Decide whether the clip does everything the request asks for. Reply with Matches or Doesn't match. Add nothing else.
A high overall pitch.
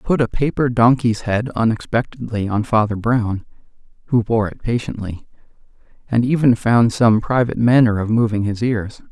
Doesn't match